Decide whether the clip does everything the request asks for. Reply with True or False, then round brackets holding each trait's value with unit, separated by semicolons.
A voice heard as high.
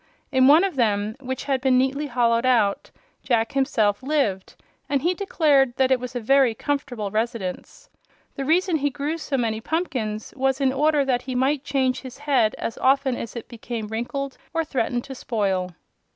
True (260 Hz)